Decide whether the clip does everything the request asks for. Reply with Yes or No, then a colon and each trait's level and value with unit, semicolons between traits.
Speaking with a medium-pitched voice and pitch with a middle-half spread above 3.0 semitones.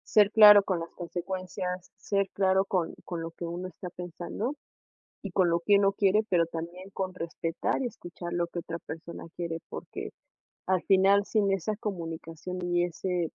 No: medium, 180 Hz; narrow, 2.4 semitones